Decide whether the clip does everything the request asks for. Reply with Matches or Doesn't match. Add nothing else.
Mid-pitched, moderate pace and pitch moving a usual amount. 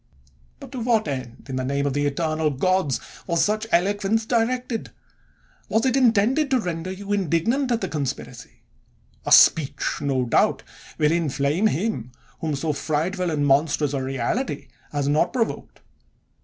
Doesn't match